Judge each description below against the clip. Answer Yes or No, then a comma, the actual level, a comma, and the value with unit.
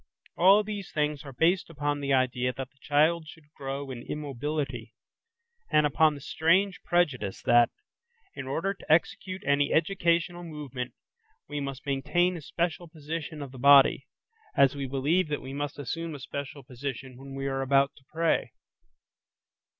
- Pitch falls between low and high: Yes, medium, 145 Hz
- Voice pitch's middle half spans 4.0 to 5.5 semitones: No, average, 3.5 semitones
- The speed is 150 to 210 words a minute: Yes, average, 160 wpm